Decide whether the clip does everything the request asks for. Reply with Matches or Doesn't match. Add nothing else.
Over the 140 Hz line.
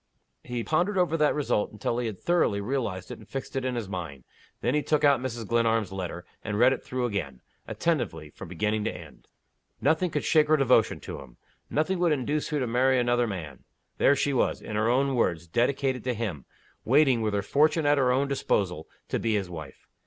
Doesn't match